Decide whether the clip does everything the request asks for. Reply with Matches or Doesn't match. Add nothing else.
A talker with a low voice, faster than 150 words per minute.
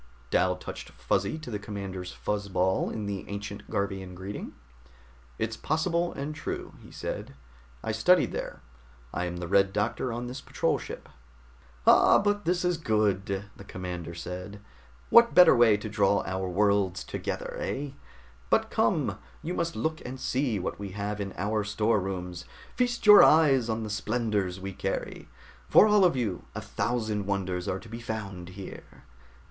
Matches